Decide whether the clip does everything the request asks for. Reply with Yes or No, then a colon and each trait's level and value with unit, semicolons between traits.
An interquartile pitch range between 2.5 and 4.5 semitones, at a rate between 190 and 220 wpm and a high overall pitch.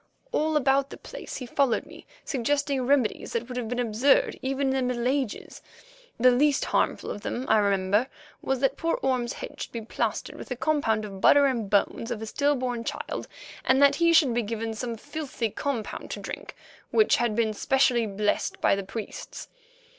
Yes: average, 3.7 semitones; average, 200 wpm; very high, 250 Hz